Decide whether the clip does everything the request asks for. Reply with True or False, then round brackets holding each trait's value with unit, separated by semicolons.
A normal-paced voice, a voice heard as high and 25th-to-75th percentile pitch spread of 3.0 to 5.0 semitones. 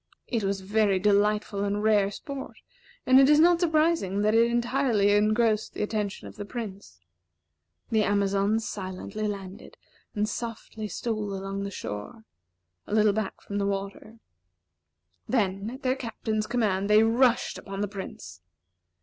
False (150 wpm; 210 Hz; 2.5 semitones)